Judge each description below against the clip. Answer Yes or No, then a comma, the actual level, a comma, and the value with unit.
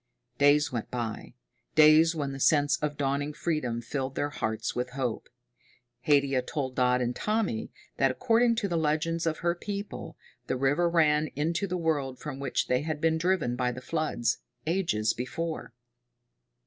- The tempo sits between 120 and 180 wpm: Yes, average, 160 wpm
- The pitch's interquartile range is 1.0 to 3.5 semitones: No, average, 4.4 semitones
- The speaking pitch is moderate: Yes, medium, 145 Hz